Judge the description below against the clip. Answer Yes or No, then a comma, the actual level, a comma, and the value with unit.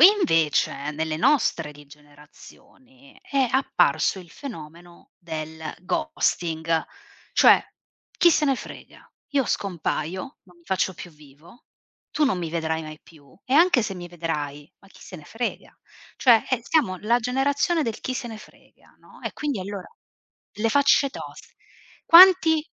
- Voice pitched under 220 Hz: Yes, high, 190 Hz